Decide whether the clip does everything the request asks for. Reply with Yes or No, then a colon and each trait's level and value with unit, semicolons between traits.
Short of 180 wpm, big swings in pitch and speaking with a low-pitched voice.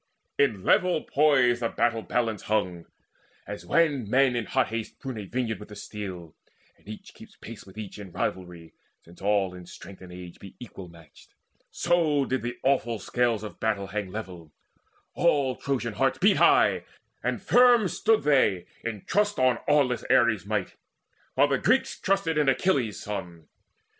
Yes: average, 170 wpm; wide, 5.9 semitones; low, 115 Hz